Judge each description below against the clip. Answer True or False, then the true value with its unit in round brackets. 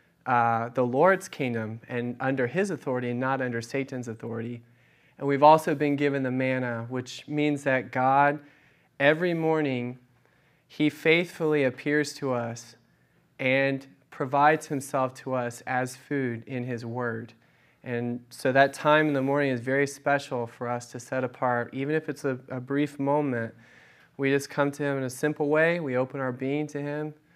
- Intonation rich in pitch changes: False (2.9 semitones)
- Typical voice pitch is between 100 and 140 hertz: True (135 Hz)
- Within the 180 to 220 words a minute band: False (170 wpm)